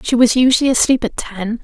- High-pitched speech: Yes, high, 240 Hz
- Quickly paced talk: Yes, fast, 220 wpm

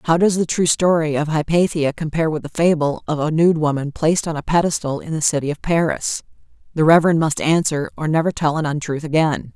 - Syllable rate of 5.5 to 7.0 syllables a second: Yes, 5.9 syllables/s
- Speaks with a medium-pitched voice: Yes, medium, 155 Hz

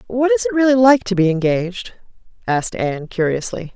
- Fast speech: No, average, 175 wpm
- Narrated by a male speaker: No, female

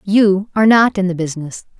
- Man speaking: No, female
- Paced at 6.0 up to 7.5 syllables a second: No, 5.8 syllables/s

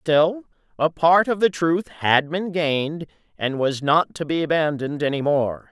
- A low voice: No, medium, 160 Hz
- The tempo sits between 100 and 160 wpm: No, average, 180 wpm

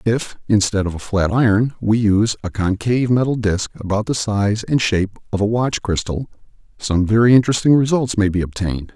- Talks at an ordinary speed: Yes, average, 190 wpm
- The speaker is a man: Yes, male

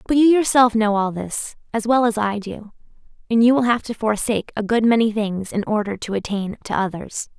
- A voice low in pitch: No, high, 220 Hz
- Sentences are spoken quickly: Yes, fast, 220 wpm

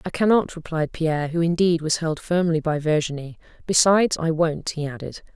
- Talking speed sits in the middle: Yes, average, 180 wpm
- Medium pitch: Yes, medium, 165 Hz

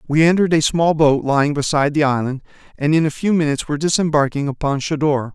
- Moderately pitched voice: Yes, medium, 150 Hz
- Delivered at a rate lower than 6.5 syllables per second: No, 6.6 syllables/s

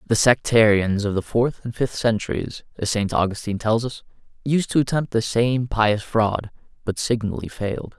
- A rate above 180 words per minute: No, average, 175 wpm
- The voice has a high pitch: No, low, 115 Hz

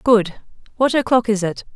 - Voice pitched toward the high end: Yes, high, 220 Hz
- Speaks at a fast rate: No, average, 170 wpm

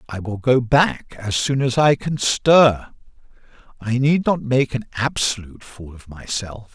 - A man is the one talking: Yes, male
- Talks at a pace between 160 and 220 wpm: Yes, average, 170 wpm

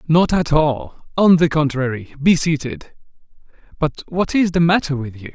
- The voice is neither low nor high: Yes, medium, 155 Hz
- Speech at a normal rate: Yes, average, 170 wpm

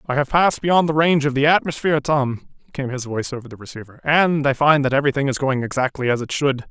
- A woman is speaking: No, male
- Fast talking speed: Yes, fast, 240 wpm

